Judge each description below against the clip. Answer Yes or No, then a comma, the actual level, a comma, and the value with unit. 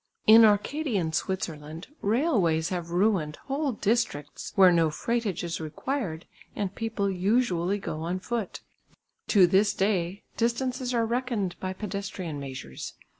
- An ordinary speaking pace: No, slow, 125 wpm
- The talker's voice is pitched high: Yes, high, 195 Hz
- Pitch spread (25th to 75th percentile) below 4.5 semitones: No, average, 5.2 semitones